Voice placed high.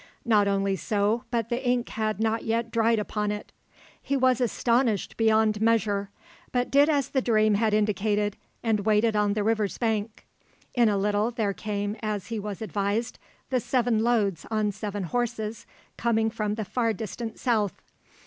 Yes: high, 220 Hz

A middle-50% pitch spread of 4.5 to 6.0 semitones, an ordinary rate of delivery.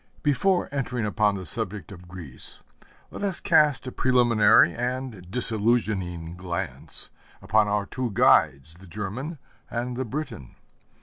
No: wide, 5.5 semitones; slow, 130 wpm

